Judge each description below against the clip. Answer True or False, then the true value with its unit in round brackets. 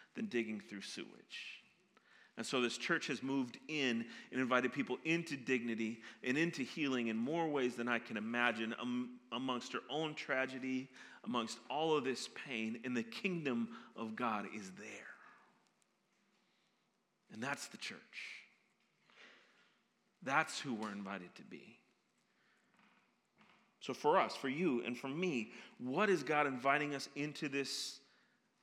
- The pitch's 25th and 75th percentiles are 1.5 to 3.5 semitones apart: False (3.9 semitones)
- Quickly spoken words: False (145 wpm)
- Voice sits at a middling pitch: False (130 Hz)